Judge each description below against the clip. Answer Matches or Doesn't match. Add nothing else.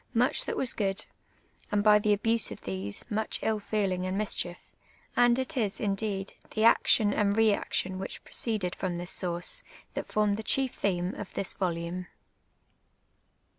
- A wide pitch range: Doesn't match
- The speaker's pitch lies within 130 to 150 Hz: Doesn't match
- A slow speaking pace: Doesn't match